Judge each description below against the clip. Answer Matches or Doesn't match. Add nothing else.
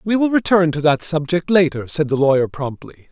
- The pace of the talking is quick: Matches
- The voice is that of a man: Matches